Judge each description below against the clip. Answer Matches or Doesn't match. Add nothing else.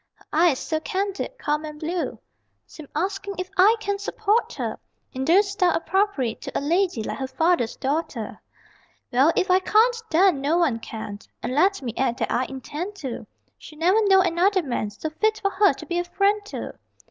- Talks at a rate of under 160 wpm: Doesn't match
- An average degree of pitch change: Doesn't match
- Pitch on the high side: Matches